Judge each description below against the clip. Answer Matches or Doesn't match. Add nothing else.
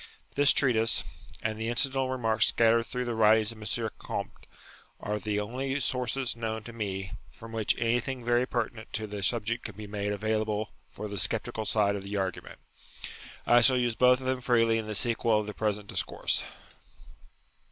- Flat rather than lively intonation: Matches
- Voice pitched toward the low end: Matches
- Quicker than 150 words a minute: Matches